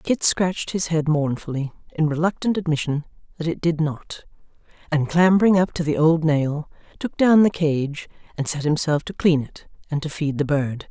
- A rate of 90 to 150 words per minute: No, average, 185 wpm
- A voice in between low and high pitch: Yes, medium, 160 Hz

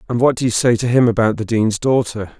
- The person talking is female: No, male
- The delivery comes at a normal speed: No, fast, 275 wpm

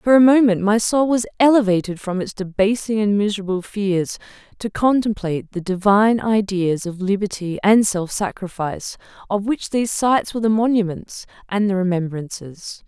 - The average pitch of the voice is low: No, high, 205 Hz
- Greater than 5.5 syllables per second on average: No, 5.2 syllables/s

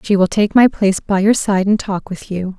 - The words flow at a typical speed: No, fast, 280 wpm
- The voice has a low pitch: No, high, 195 Hz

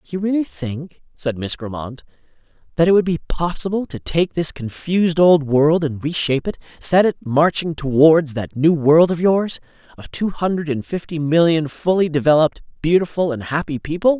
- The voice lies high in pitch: No, medium, 160 Hz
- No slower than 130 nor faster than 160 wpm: No, average, 170 wpm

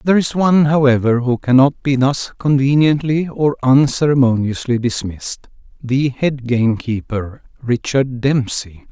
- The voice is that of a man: Yes, male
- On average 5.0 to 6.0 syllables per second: No, 4.5 syllables/s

